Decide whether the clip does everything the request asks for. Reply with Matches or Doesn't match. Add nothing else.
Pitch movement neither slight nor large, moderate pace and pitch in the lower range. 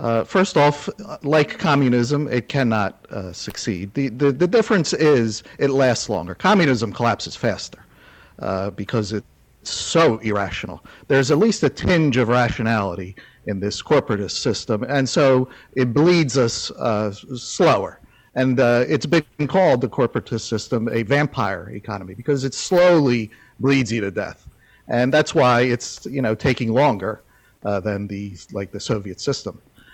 Matches